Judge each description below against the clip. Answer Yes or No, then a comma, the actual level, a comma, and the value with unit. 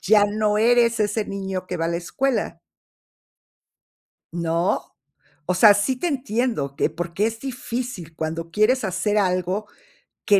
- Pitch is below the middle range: No, high, 205 Hz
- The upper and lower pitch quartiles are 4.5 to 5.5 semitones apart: Yes, average, 4.9 semitones